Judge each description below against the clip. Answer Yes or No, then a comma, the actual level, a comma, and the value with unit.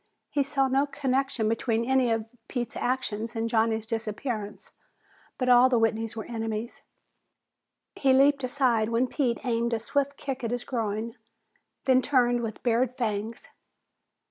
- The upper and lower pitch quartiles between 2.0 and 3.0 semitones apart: Yes, narrow, 2.6 semitones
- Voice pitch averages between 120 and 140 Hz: No, high, 240 Hz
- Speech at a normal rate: Yes, average, 145 wpm